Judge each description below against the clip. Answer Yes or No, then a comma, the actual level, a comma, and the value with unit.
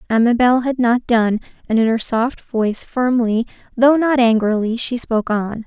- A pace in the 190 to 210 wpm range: No, average, 170 wpm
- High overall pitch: Yes, high, 235 Hz